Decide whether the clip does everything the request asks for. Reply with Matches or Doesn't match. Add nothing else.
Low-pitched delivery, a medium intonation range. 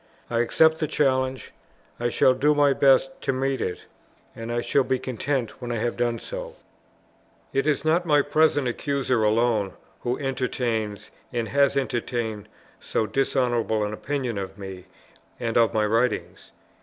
Matches